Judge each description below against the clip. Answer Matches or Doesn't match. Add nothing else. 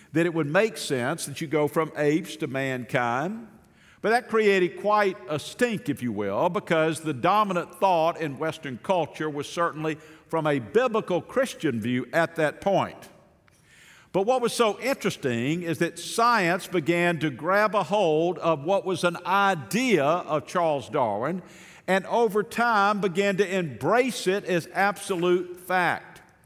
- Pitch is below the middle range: Doesn't match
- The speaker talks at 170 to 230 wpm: Doesn't match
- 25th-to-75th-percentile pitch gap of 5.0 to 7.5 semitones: Doesn't match